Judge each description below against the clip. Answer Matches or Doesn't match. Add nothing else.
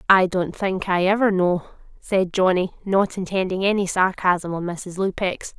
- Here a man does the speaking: Doesn't match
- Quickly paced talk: Doesn't match